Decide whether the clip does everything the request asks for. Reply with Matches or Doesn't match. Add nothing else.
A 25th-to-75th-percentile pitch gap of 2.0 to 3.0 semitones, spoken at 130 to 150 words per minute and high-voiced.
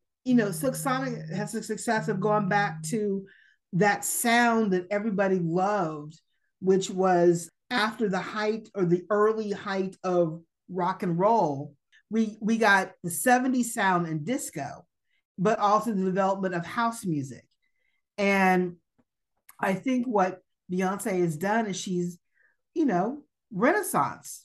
Doesn't match